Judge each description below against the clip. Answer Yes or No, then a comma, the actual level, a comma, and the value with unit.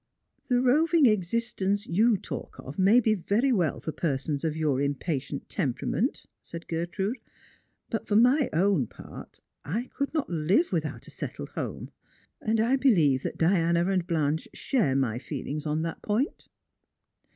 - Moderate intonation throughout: No, wide, 6.9 semitones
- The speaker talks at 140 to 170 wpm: Yes, average, 160 wpm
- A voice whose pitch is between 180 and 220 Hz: Yes, medium, 185 Hz